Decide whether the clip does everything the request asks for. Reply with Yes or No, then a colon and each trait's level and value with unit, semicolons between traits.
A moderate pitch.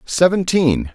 Yes: medium, 155 Hz